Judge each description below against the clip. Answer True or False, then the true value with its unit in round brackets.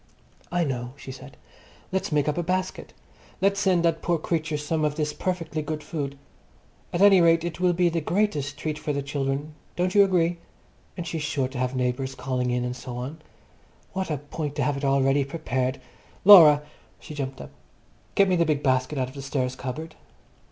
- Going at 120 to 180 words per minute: False (200 wpm)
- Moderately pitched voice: True (150 Hz)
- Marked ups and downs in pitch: False (3.9 semitones)